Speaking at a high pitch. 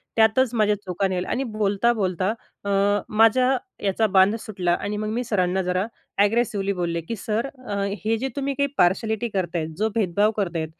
Yes: high, 210 Hz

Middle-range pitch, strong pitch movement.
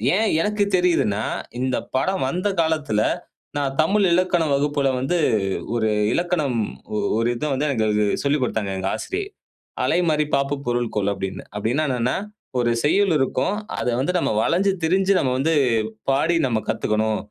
Yes: medium, 145 Hz; wide, 6.9 semitones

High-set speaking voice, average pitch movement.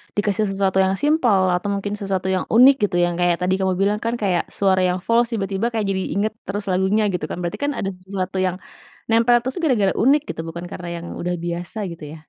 Yes: high, 195 Hz; average, 3.1 semitones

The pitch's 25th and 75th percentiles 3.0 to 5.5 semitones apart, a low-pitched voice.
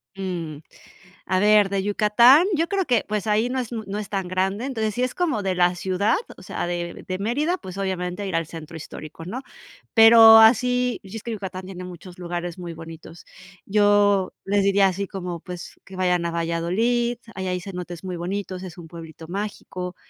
No: average, 3.5 semitones; high, 195 Hz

